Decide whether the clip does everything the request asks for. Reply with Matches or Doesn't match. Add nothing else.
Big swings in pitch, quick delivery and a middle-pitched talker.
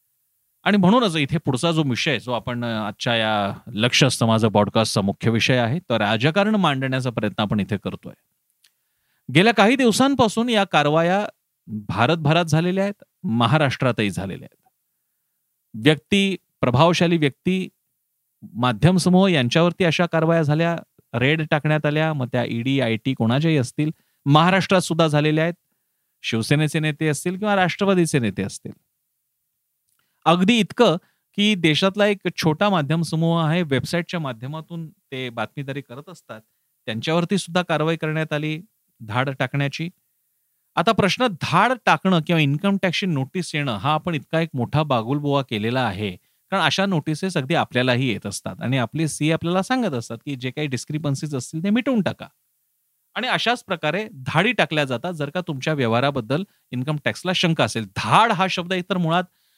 Matches